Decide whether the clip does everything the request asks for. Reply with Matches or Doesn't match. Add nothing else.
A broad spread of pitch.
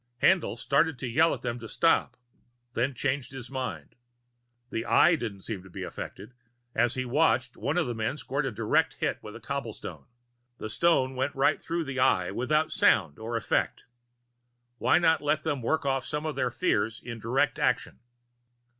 Doesn't match